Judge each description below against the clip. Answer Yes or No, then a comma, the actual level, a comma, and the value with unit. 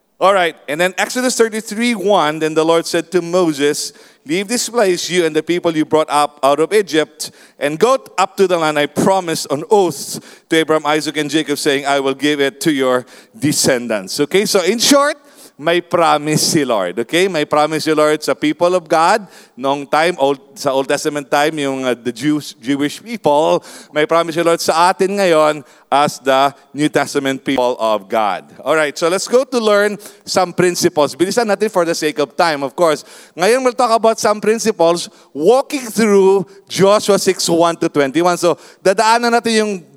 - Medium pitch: Yes, medium, 170 Hz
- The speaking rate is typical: Yes, average, 195 wpm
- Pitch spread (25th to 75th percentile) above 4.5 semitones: Yes, average, 5.0 semitones